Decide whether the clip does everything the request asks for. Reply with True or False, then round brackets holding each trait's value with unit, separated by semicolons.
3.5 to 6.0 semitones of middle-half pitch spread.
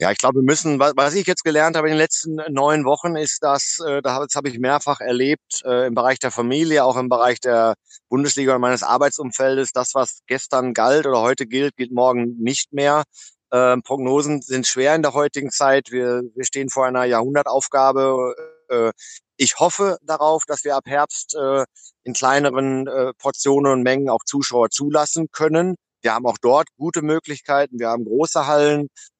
False (2.5 semitones)